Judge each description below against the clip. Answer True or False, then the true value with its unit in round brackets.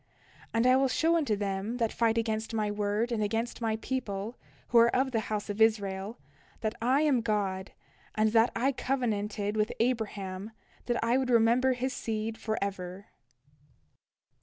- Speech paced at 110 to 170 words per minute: True (160 wpm)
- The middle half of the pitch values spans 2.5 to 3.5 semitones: True (2.8 semitones)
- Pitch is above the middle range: True (225 Hz)